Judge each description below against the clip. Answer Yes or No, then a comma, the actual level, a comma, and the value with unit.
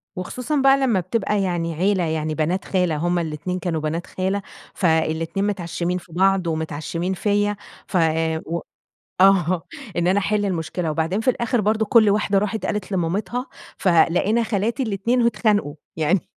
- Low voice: No, medium, 185 Hz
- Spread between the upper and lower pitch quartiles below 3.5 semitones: No, average, 3.8 semitones